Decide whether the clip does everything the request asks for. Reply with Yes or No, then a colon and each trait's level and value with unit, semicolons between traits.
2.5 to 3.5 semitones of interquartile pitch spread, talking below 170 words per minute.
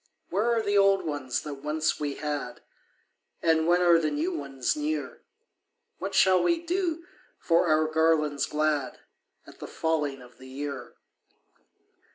No: average, 4.7 semitones; average, 150 wpm